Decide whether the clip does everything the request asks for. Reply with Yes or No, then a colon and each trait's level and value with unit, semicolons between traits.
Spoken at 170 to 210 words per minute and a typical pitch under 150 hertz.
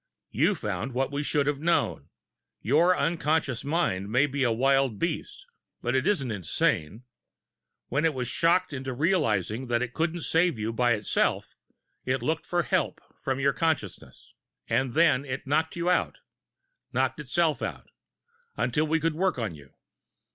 No: average, 160 wpm; low, 135 Hz